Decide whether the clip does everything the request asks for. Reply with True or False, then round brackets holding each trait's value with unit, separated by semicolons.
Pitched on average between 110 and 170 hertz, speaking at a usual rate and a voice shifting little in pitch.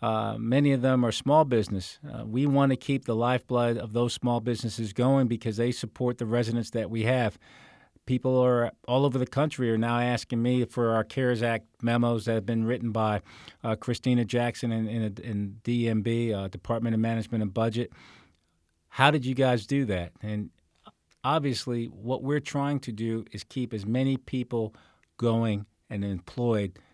True (115 Hz; 180 wpm; 2.3 semitones)